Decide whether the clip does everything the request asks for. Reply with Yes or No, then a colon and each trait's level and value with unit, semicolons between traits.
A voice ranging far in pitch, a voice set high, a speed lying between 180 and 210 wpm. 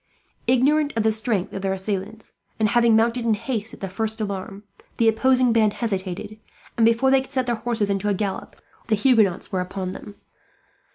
No: average, 3.1 semitones; high, 220 Hz; average, 190 wpm